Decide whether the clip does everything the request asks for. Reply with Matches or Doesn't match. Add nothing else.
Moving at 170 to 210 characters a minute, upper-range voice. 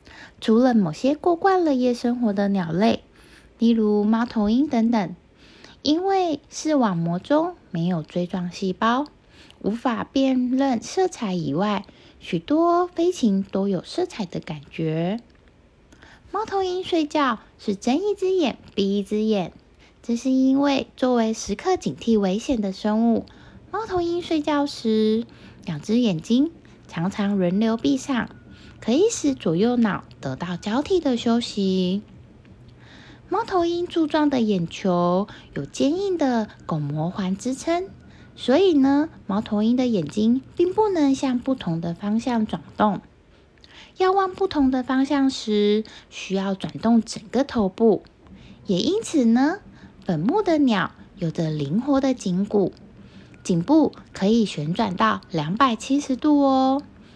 Matches